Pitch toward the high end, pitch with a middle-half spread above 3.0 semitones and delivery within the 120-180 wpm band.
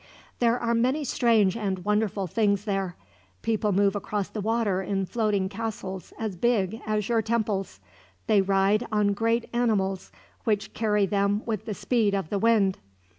No: high, 210 Hz; narrow, 2.5 semitones; average, 160 wpm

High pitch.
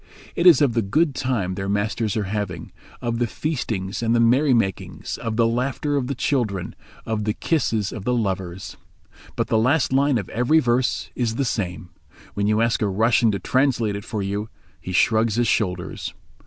No: low, 115 Hz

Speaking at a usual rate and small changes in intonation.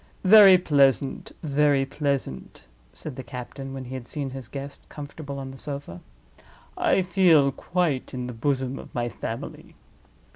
Yes: average, 150 wpm; narrow, 2.3 semitones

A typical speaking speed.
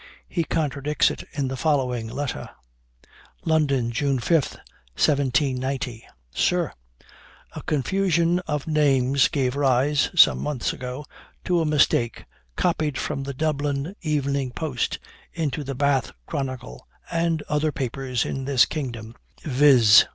No: slow, 120 wpm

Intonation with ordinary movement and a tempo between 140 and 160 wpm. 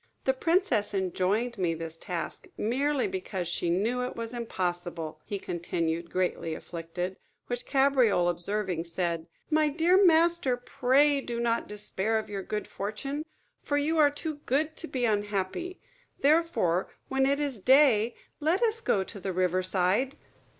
No: wide, 7.8 semitones; average, 150 wpm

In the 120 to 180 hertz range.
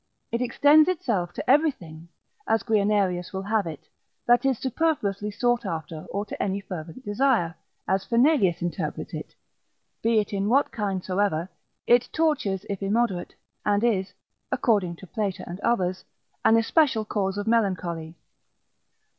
No: high, 205 Hz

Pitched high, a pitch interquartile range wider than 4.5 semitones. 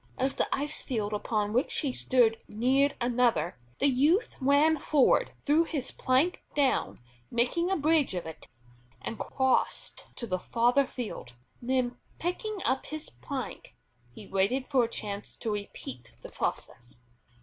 Yes: very high, 255 Hz; average, 5.0 semitones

